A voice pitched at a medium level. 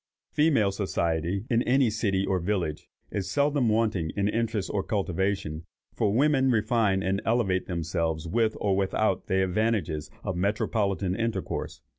No: low, 100 Hz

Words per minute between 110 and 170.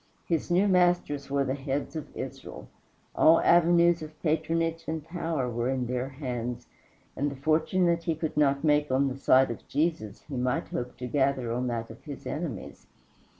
No: average, 185 wpm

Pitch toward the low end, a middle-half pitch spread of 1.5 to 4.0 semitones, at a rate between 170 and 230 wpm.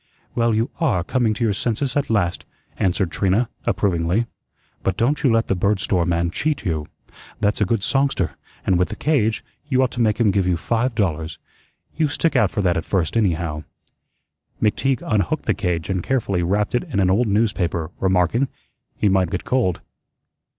No: low, 100 Hz; average, 4.8 semitones; average, 185 wpm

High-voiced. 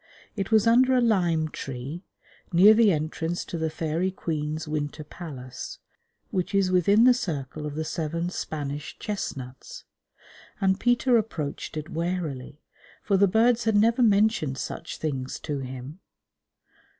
No: medium, 170 Hz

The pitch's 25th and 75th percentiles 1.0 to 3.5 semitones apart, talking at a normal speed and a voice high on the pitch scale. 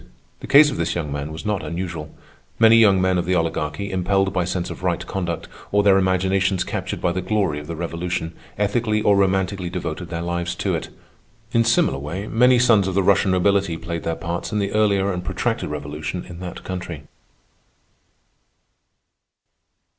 No: average, 2.8 semitones; average, 180 wpm; very low, 95 Hz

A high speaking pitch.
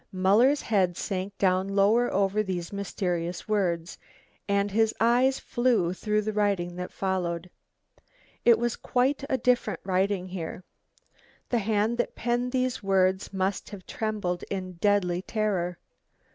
Yes: high, 200 Hz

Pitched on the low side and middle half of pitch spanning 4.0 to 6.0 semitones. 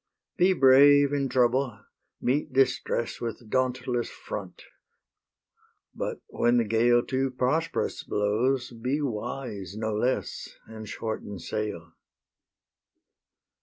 No: low, 125 Hz; average, 3.3 semitones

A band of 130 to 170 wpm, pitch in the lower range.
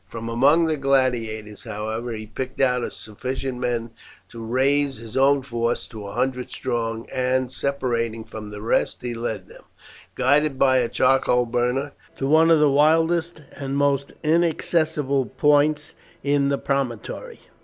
Yes: average, 150 wpm; low, 130 Hz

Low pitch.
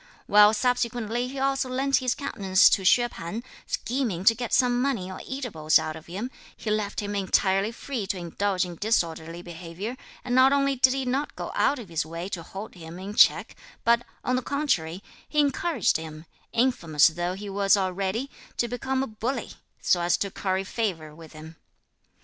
No: high, 205 Hz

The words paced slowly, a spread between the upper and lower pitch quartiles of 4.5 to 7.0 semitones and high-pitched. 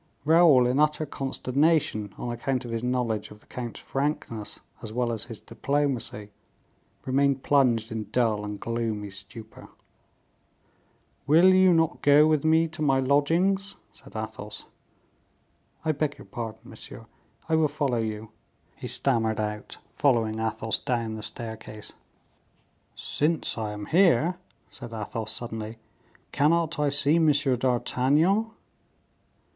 No: slow, 130 wpm; average, 5.2 semitones; low, 125 Hz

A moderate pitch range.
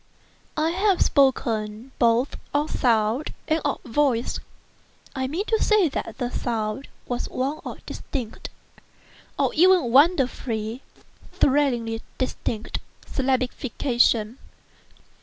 Yes: average, 4.1 semitones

